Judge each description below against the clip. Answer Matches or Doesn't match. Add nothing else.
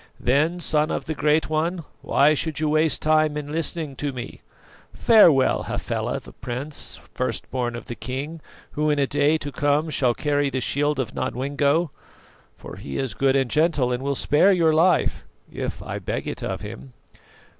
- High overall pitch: Doesn't match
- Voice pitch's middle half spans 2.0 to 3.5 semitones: Matches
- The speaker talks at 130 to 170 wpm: Doesn't match